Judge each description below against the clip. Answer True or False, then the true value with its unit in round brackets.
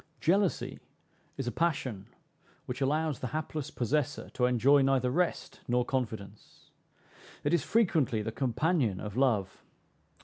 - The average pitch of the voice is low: True (130 Hz)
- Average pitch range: True (4.5 semitones)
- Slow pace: True (130 wpm)